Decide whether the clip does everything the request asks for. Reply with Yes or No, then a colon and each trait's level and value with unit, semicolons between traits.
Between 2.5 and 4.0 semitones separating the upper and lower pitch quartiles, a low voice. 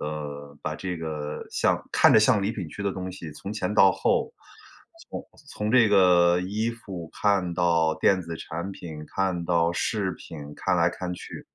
Yes: average, 3.4 semitones; very low, 90 Hz